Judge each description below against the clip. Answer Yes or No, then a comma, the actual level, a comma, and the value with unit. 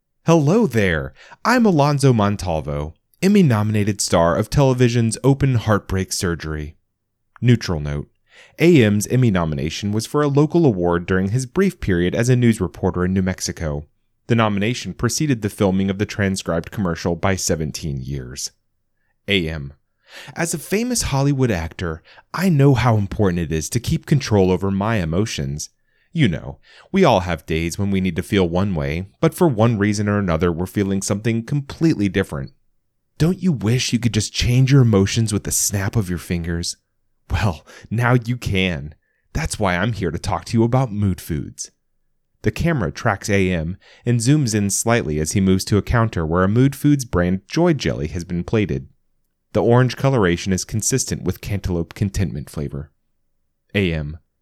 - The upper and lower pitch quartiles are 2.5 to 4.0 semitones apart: No, wide, 5.6 semitones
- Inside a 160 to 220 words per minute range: Yes, average, 170 wpm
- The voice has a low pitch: Yes, low, 100 Hz